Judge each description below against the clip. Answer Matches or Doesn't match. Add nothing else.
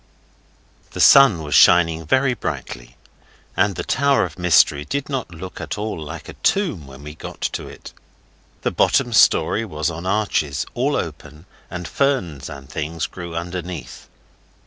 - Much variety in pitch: Matches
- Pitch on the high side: Doesn't match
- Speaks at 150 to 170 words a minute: Matches